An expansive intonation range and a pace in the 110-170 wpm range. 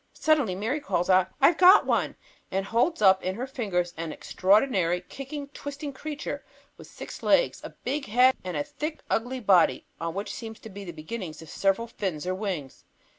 No: wide, 6.7 semitones; average, 185 wpm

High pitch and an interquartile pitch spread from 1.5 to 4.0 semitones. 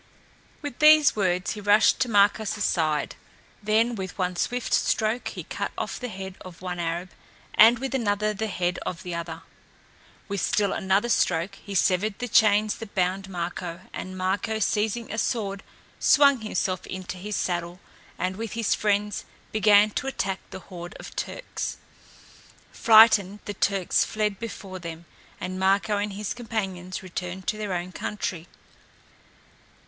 Yes: high, 200 Hz; average, 2.9 semitones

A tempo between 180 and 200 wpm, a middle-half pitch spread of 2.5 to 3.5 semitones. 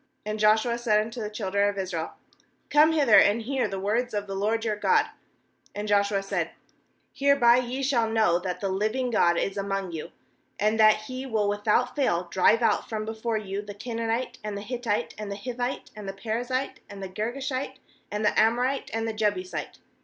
Yes: average, 190 wpm; average, 3.1 semitones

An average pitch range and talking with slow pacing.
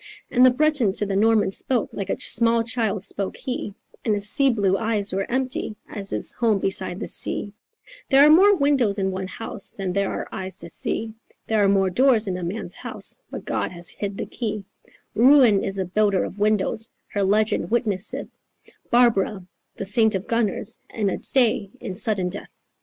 No: average, 3.3 semitones; average, 190 wpm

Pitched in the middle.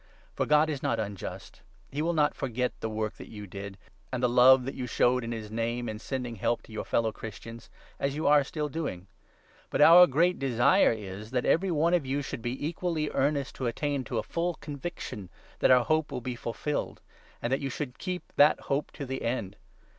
No: low, 130 Hz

